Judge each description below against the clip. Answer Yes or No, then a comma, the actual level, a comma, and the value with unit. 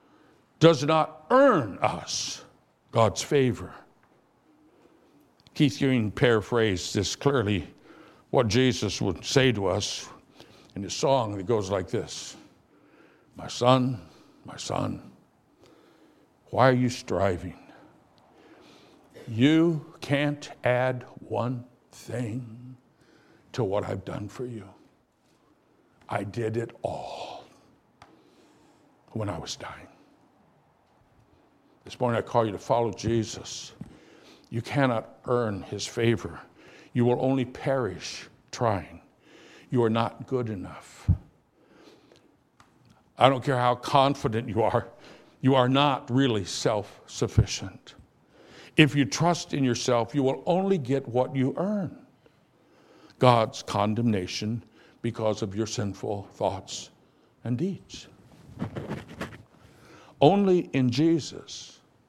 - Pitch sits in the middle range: No, low, 125 Hz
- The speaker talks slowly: Yes, slow, 105 wpm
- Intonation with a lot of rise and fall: No, average, 3.6 semitones